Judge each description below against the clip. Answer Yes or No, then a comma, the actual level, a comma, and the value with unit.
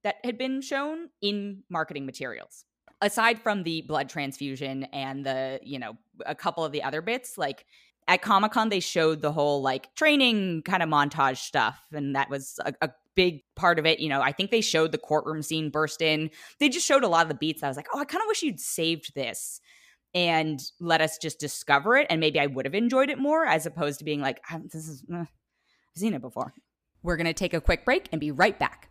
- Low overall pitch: No, medium, 160 Hz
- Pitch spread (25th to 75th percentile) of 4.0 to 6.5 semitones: Yes, wide, 5.6 semitones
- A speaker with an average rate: No, fast, 235 wpm